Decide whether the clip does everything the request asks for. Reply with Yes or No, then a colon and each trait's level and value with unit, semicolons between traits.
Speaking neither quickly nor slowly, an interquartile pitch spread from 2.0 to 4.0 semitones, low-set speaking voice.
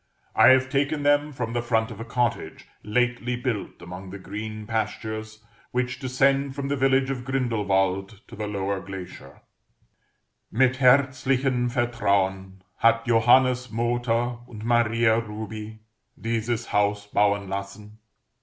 No: slow, 130 wpm; average, 3.4 semitones; low, 115 Hz